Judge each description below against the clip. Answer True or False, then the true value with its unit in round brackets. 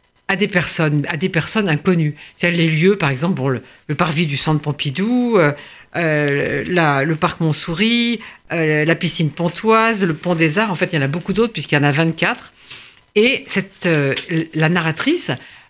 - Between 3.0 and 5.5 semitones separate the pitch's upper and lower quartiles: True (4.3 semitones)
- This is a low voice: False (165 Hz)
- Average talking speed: True (195 wpm)